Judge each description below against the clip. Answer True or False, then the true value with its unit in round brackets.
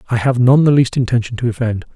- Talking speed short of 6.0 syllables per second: False (6.7 syllables/s)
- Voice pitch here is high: False (120 Hz)